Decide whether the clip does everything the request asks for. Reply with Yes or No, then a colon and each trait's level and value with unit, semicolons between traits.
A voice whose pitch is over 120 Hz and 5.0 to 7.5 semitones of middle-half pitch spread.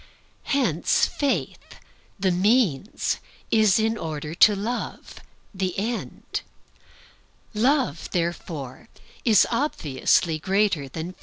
Yes: high, 190 Hz; wide, 5.6 semitones